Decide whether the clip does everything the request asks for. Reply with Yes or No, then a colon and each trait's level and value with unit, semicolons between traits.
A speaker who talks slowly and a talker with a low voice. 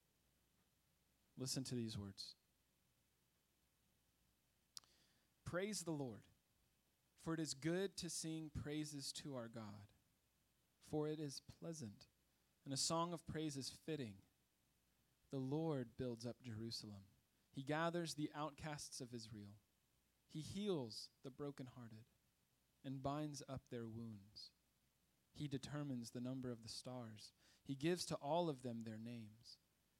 Yes: slow, 125 wpm; low, 130 Hz